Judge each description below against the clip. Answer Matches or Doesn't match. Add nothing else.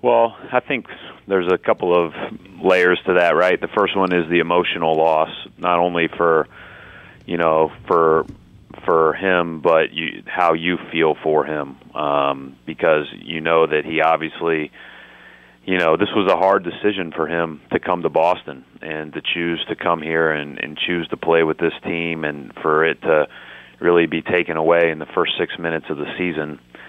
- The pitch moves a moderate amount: Doesn't match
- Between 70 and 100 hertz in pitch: Matches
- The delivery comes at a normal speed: Matches